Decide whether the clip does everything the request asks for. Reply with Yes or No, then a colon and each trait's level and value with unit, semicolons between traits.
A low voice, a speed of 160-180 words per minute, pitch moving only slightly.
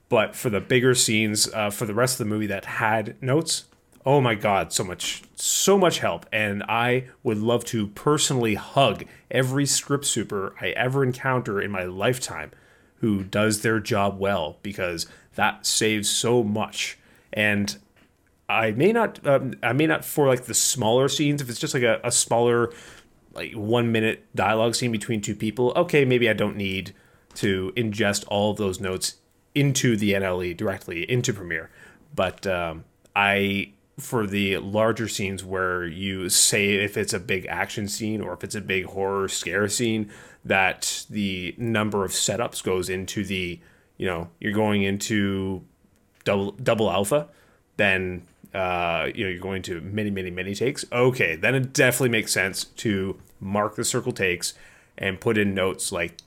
No: low, 105 Hz; average, 170 wpm; average, 3.8 semitones